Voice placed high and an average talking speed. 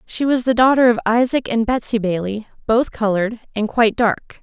Yes: high, 230 Hz; average, 190 wpm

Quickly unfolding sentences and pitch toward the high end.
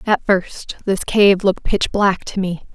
No: average, 195 wpm; high, 195 Hz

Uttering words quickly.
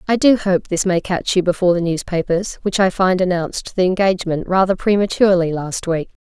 No: average, 190 wpm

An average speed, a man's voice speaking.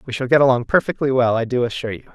No: fast, 280 wpm; male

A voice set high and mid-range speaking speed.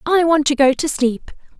No: very high, 290 Hz; fast, 225 wpm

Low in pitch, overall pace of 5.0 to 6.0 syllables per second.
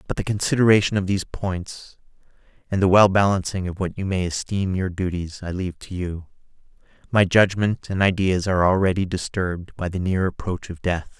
Yes: very low, 95 Hz; 5.5 syllables/s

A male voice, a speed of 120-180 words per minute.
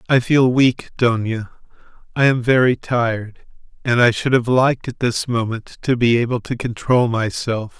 Yes: male; average, 170 wpm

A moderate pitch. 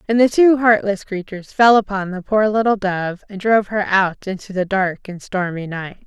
No: high, 200 Hz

